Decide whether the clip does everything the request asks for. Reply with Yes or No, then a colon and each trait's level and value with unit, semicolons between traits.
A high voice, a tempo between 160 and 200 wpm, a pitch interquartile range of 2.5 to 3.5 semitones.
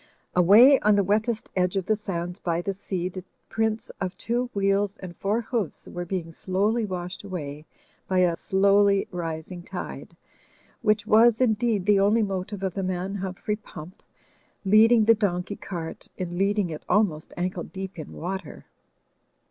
Yes: high, 195 Hz; average, 165 wpm; average, 2.8 semitones